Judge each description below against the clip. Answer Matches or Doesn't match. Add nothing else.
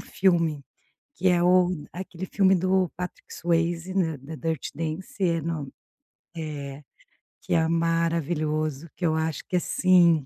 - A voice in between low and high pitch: Matches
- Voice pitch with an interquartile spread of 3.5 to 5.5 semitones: Doesn't match